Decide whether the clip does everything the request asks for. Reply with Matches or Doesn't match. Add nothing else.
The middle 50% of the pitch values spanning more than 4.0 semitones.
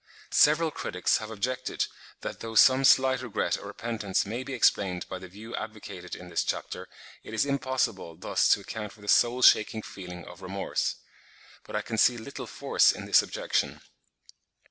Matches